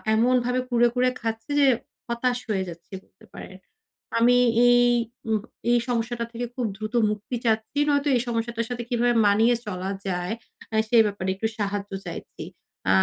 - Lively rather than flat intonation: No, narrow, 2.6 semitones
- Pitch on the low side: No, high, 230 Hz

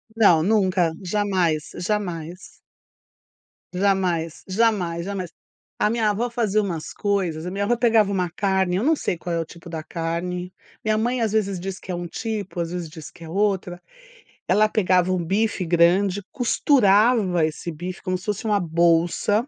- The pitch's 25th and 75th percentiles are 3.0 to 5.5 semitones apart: Yes, average, 3.4 semitones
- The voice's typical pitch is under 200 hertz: Yes, medium, 185 Hz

